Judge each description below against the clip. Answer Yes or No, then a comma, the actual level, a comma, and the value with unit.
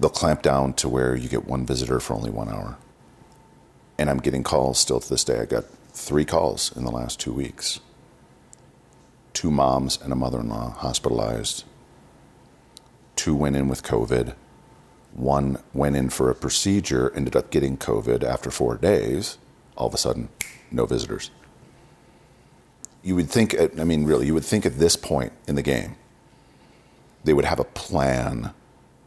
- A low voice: Yes, very low, 65 Hz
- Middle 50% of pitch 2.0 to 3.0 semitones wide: Yes, narrow, 2.6 semitones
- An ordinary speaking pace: Yes, average, 170 wpm